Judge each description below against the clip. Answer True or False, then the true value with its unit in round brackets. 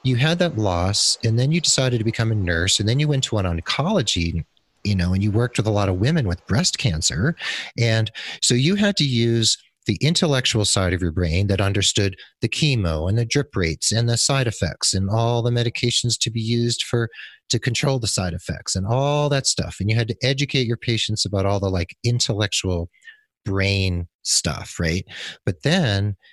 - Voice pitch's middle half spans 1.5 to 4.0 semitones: False (4.8 semitones)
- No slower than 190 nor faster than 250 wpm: True (205 wpm)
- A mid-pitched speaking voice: False (115 Hz)